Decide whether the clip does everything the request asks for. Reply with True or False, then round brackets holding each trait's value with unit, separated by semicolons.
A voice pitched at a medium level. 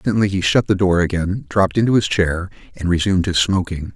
False (90 Hz)